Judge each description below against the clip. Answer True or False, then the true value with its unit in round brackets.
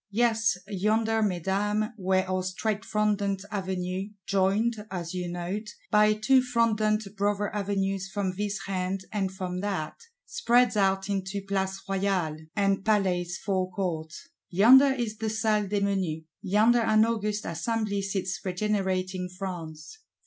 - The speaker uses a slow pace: True (130 wpm)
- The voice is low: False (195 Hz)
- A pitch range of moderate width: False (2.2 semitones)